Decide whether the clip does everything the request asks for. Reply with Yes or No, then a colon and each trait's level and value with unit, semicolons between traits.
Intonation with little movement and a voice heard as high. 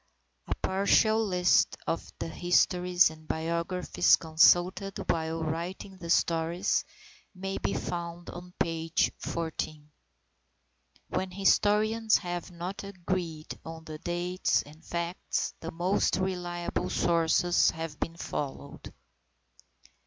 No: narrow, 2.1 semitones; medium, 175 Hz